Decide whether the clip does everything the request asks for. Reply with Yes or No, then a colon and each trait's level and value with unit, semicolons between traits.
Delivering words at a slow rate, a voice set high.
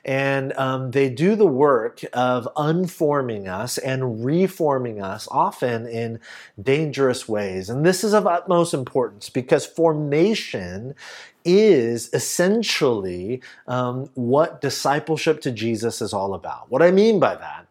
No: slow, 130 wpm; low, 135 Hz